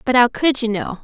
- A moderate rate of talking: No, fast, 290 wpm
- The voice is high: Yes, high, 240 Hz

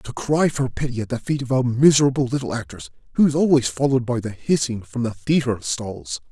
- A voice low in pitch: Yes, low, 125 Hz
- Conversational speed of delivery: No, fast, 210 wpm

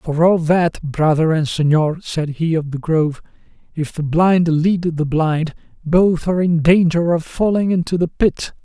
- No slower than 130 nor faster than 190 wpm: Yes, average, 180 wpm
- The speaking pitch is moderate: Yes, medium, 165 Hz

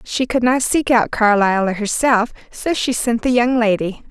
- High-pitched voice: Yes, high, 230 Hz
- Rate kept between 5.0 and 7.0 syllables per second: No, 4.5 syllables/s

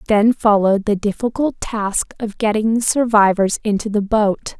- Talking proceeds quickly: No, average, 155 wpm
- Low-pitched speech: No, high, 215 Hz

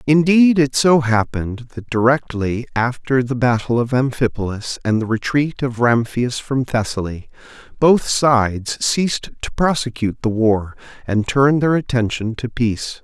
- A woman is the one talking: No, male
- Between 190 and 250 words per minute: No, average, 145 wpm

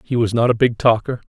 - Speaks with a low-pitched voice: Yes, low, 115 Hz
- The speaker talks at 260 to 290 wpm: Yes, fast, 275 wpm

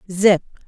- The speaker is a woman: Yes, female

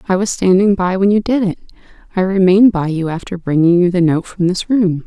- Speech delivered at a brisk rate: Yes, fast, 235 wpm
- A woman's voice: Yes, female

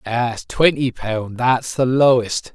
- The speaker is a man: Yes, male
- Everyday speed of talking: No, slow, 120 wpm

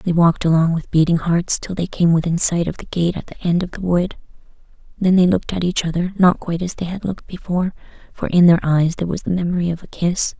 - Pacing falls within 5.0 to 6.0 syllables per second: No, 6.2 syllables/s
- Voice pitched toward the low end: No, medium, 175 Hz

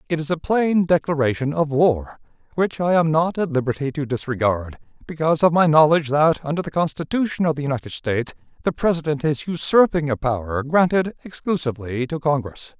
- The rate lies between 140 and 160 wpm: No, average, 175 wpm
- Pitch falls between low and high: Yes, medium, 150 Hz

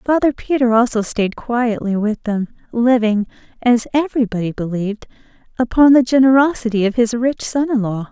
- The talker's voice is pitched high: Yes, high, 235 Hz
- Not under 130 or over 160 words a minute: Yes, average, 150 wpm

